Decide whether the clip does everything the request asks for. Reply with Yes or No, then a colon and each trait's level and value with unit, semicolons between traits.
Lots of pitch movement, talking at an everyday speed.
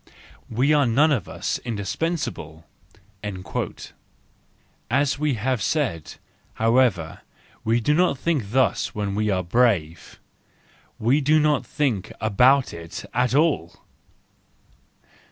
No: wide, 6.3 semitones; slow, 110 wpm